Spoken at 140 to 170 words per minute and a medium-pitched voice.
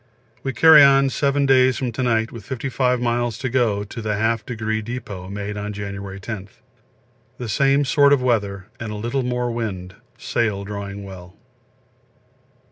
No: average, 165 wpm; low, 115 Hz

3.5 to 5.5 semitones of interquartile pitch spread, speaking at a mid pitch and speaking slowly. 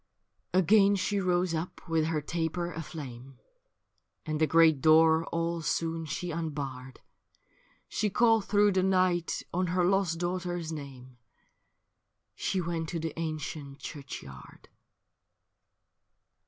No: average, 2.8 semitones; medium, 165 Hz; slow, 115 wpm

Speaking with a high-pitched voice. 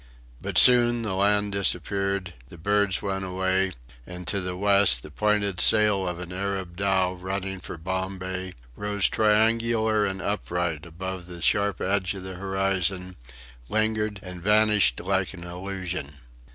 No: very low, 95 Hz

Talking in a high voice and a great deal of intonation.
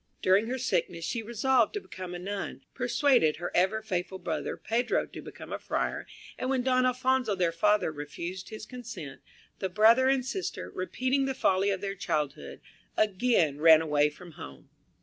Yes: high, 200 Hz; wide, 6.3 semitones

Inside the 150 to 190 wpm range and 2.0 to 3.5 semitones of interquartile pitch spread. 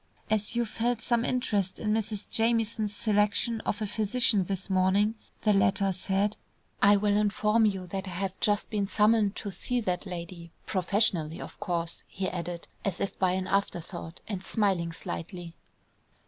Yes: average, 160 wpm; narrow, 2.6 semitones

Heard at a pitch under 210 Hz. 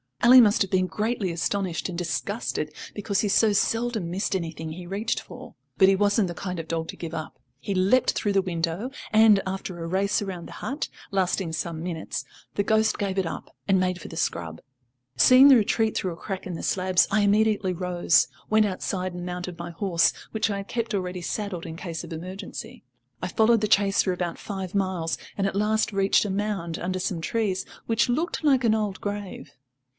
Yes: high, 190 Hz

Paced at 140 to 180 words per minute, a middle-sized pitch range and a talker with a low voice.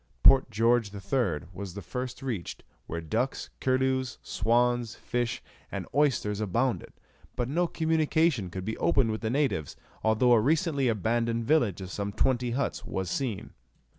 Yes: average, 150 wpm; average, 4.2 semitones; low, 120 Hz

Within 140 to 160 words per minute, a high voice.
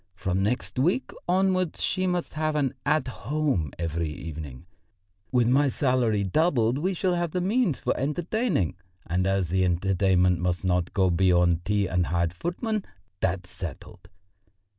No: average, 150 wpm; low, 105 Hz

